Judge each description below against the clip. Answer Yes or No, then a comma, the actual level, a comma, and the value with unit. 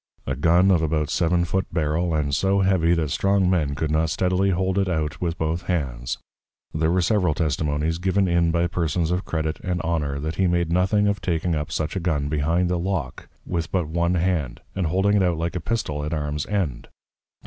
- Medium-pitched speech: No, very low, 85 Hz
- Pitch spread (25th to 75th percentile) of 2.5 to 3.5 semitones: Yes, average, 2.9 semitones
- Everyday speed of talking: No, fast, 210 wpm